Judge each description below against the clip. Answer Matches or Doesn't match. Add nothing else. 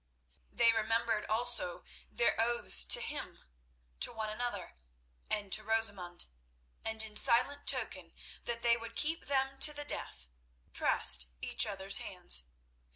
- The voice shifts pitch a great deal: Doesn't match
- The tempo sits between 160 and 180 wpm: Doesn't match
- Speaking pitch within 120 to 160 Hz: Doesn't match